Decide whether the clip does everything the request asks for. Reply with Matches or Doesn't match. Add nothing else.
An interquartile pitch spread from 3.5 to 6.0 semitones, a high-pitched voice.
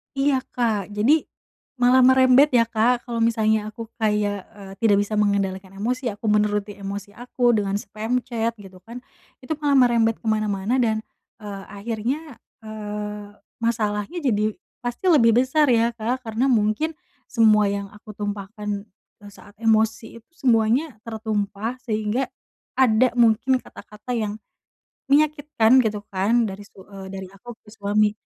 Doesn't match